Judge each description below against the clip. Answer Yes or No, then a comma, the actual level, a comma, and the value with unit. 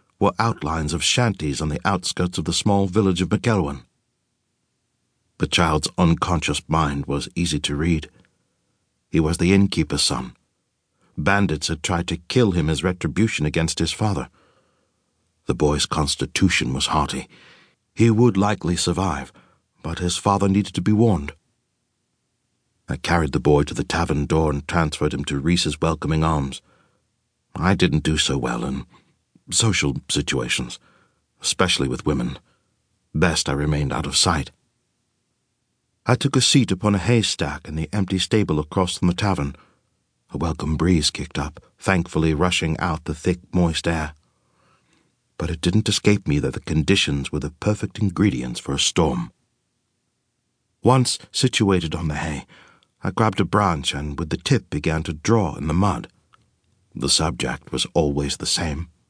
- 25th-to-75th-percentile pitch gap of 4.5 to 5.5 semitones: Yes, average, 5.0 semitones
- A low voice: Yes, very low, 85 Hz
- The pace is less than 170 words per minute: Yes, average, 155 wpm